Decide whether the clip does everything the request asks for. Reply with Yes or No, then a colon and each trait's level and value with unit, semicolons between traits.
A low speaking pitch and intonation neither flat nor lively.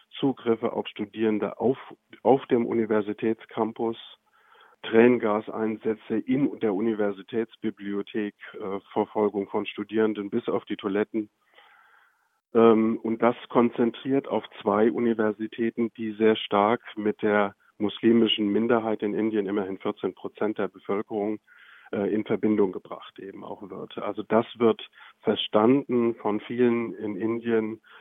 No: low, 110 Hz; narrow, 1.6 semitones